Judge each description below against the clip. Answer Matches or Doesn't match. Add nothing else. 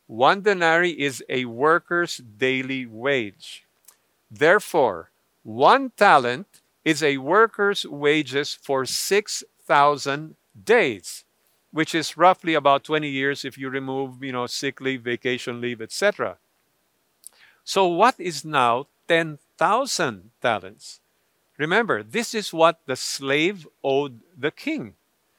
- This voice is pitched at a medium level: Matches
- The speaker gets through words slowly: Matches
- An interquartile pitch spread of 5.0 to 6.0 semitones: Doesn't match